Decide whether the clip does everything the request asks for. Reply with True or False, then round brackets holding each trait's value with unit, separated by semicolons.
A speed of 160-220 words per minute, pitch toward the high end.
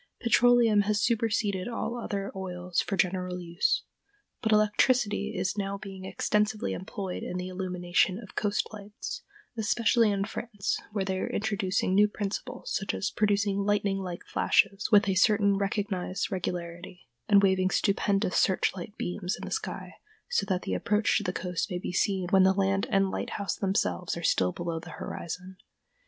True (165 wpm; 195 Hz)